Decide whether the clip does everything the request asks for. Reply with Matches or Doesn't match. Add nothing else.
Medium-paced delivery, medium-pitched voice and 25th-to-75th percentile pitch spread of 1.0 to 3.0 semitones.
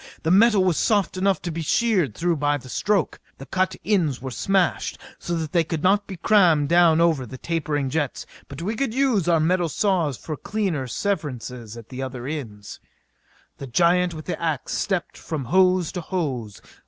Doesn't match